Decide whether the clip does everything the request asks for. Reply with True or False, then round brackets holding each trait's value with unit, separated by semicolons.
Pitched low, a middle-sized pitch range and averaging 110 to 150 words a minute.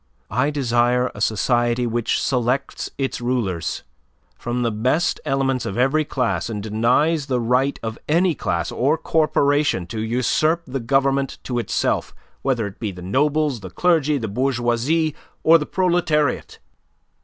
True (125 Hz; 4.0 semitones; 145 wpm)